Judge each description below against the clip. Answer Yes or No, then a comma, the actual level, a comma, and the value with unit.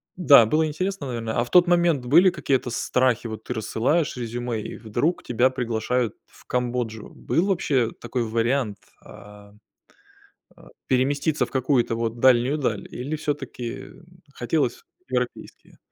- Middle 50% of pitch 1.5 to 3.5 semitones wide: No, average, 4.0 semitones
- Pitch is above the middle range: No, low, 125 Hz